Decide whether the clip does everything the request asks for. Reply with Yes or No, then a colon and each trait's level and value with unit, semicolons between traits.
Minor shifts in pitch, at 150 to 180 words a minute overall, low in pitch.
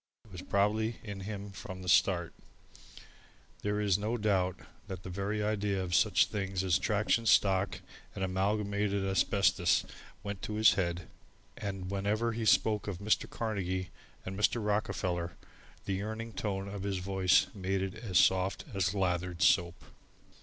Yes: narrow, 2.1 semitones; average, 155 wpm; low, 100 Hz